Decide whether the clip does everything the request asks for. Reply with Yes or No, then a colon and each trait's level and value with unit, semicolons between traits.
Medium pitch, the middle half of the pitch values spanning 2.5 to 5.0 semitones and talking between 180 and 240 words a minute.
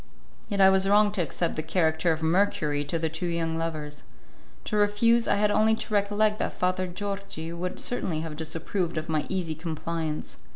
Yes: medium, 175 Hz; average, 4.1 semitones; average, 190 wpm